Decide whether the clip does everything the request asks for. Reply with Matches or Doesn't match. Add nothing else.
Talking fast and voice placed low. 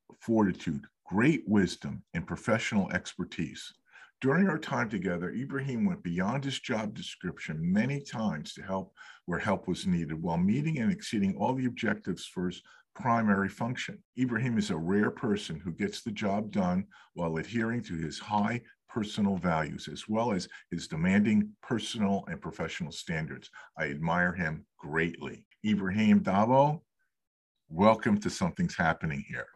Doesn't match